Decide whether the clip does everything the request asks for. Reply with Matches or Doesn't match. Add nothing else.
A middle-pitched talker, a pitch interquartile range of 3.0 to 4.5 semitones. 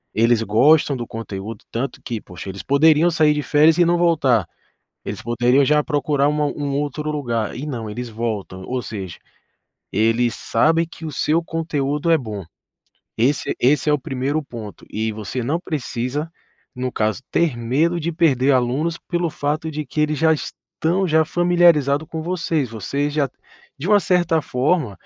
Doesn't match